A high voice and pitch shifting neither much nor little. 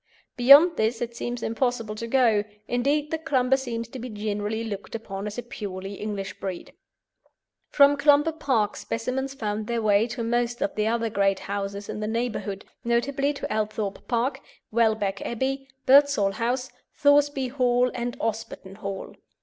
Yes: high, 235 Hz; average, 3.9 semitones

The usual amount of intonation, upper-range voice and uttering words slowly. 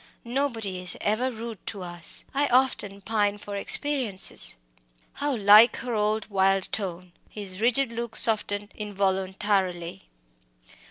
Yes: average, 3.4 semitones; high, 205 Hz; slow, 120 wpm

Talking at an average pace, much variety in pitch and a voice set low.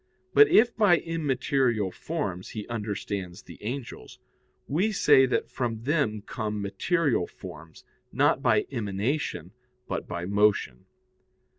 No: slow, 120 wpm; wide, 6.5 semitones; low, 115 Hz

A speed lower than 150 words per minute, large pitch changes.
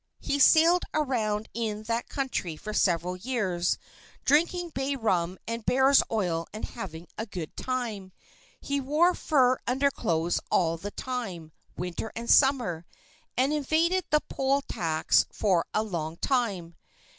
Yes: slow, 135 wpm; wide, 7.2 semitones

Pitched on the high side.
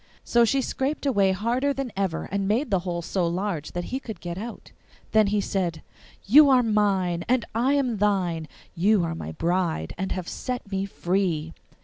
Yes: high, 195 Hz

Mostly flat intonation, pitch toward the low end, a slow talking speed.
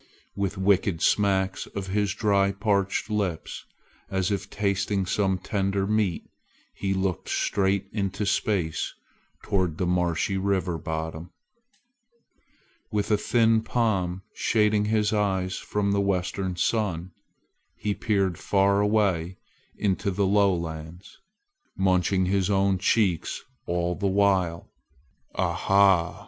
Yes: narrow, 1.8 semitones; very low, 95 Hz; slow, 115 wpm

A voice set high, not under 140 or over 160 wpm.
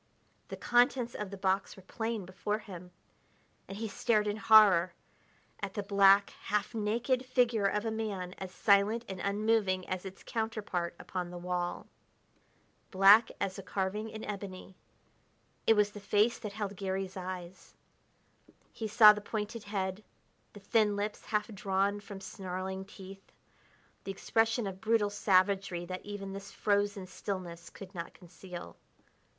Yes: high, 200 Hz; average, 150 wpm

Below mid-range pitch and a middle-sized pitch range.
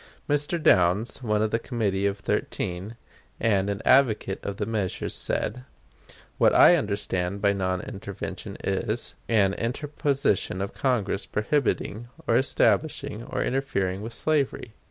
Yes: low, 105 Hz; average, 4.4 semitones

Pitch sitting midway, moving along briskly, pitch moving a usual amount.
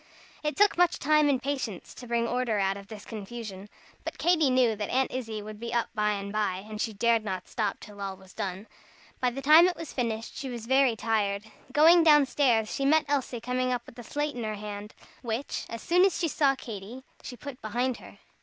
No: high, 235 Hz; fast, 225 wpm; average, 4.5 semitones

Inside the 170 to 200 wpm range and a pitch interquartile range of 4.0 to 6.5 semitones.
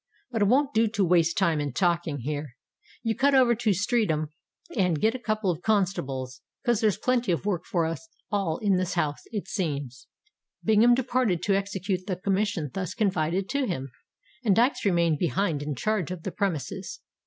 Yes: average, 180 wpm; average, 5.0 semitones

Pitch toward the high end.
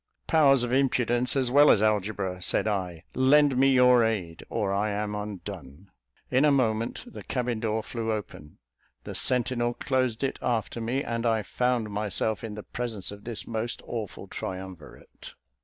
No: low, 115 Hz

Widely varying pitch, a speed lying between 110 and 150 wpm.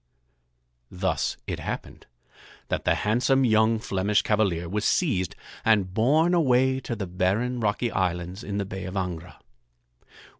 No: average, 4.7 semitones; average, 140 wpm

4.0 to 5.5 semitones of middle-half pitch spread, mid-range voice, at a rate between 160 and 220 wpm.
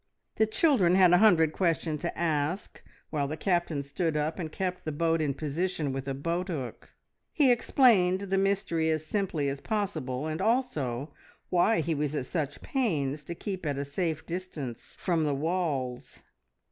Yes: average, 4.3 semitones; medium, 165 Hz; average, 170 wpm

